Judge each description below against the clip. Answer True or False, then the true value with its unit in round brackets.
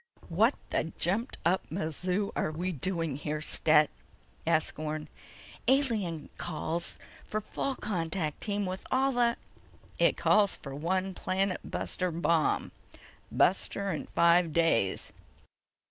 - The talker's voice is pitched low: False (175 Hz)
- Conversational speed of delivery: False (125 wpm)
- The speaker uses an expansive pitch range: False (4.1 semitones)